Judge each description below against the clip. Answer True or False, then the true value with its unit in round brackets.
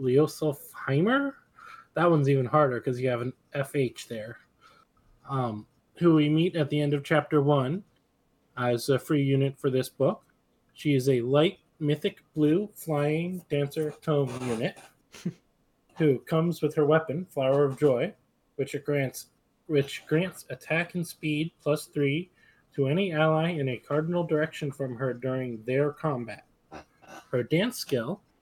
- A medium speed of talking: True (150 wpm)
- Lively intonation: False (3.0 semitones)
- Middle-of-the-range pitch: True (145 Hz)